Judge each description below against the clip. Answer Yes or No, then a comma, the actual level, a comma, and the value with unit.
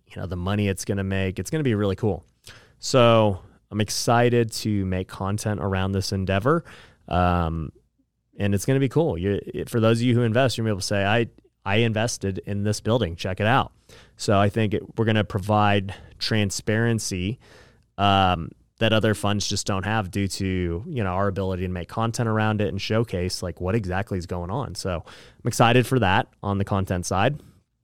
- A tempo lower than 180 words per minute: No, fast, 205 wpm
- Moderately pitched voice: No, low, 105 Hz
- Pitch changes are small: No, average, 3.0 semitones